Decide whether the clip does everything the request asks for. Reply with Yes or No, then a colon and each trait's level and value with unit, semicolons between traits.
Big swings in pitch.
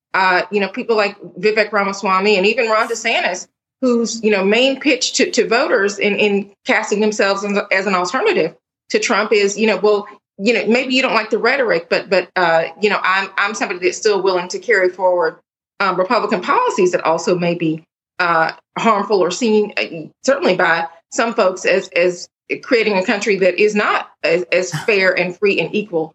No: average, 3.7 semitones